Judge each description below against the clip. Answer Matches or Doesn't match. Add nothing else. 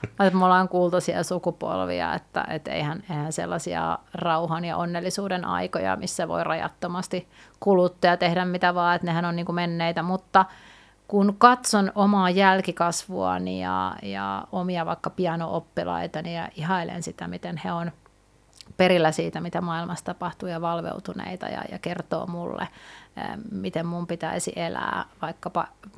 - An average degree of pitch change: Doesn't match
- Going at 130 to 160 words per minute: Matches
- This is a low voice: Doesn't match